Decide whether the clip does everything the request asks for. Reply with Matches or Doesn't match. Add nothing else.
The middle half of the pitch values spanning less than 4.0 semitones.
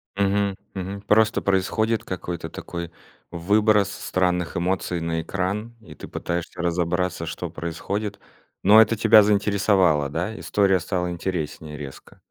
Matches